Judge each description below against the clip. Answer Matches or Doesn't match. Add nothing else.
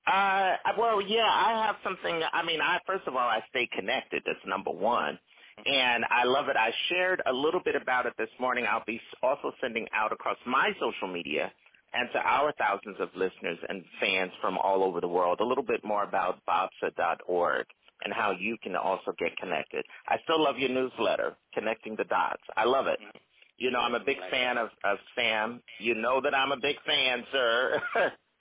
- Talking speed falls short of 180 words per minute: Doesn't match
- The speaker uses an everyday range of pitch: Doesn't match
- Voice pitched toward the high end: Doesn't match